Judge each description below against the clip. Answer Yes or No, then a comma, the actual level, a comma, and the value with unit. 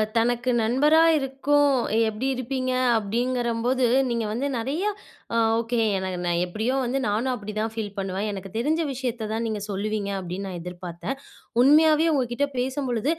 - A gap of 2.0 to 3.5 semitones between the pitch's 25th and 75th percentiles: No, average, 4.1 semitones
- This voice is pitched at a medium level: No, high, 235 Hz